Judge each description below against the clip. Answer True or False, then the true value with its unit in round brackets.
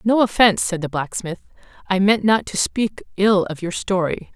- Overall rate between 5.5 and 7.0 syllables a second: False (5.0 syllables/s)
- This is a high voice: True (195 Hz)